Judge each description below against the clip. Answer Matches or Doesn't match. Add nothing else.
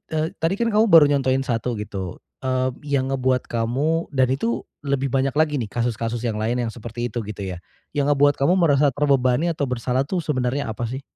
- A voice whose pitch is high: Doesn't match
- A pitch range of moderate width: Matches